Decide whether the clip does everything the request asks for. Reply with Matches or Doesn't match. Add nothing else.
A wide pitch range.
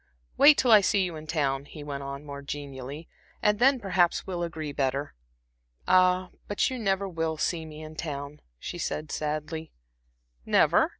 Doesn't match